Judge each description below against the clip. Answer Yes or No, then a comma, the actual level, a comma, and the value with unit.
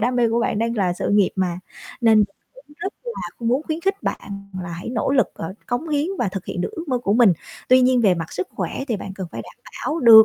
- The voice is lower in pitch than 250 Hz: Yes, high, 230 Hz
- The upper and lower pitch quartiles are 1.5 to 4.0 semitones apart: No, average, 5.3 semitones